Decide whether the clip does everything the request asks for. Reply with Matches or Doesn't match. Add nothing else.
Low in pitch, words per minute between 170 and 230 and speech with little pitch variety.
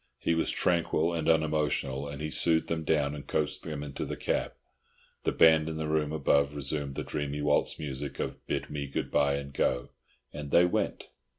Matches